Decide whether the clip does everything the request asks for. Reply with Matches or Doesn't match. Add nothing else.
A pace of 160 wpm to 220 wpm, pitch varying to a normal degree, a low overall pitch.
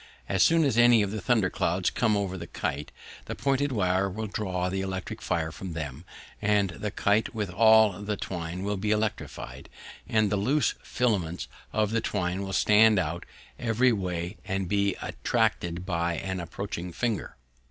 Matches